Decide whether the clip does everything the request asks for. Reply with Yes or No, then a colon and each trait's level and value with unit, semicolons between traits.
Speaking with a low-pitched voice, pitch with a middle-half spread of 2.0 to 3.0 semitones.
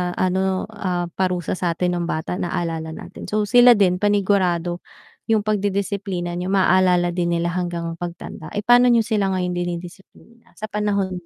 No: medium, 185 Hz; average, 2.7 semitones